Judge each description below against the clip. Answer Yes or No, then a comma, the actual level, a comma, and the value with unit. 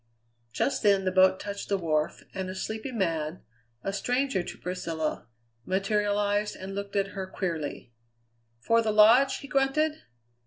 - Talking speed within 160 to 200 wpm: No, average, 150 wpm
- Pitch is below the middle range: No, high, 200 Hz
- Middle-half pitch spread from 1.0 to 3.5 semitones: Yes, average, 2.8 semitones